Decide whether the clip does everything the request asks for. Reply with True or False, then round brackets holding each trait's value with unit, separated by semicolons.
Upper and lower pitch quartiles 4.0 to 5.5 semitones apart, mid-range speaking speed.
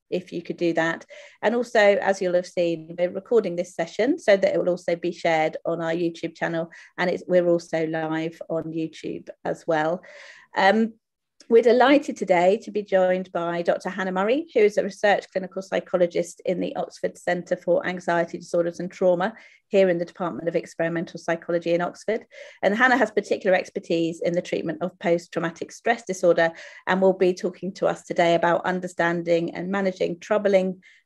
False (2.5 semitones; 185 wpm)